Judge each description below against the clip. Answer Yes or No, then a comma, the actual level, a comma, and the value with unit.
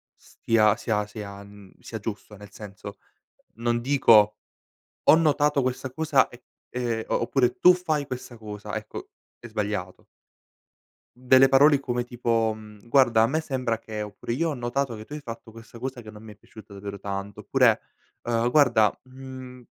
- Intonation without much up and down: No, average, 3.6 semitones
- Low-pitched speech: Yes, low, 115 Hz